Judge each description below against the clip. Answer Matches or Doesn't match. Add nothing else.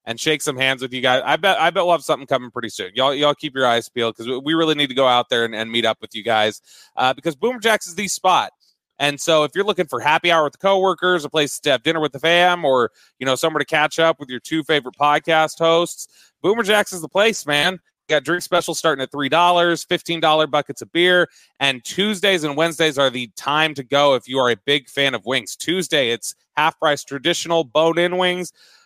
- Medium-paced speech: Doesn't match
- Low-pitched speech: Doesn't match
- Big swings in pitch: Doesn't match